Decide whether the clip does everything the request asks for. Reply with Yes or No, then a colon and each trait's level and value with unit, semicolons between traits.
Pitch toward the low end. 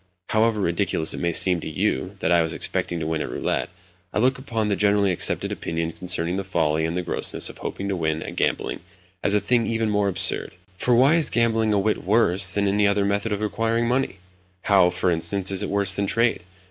Yes: low, 100 Hz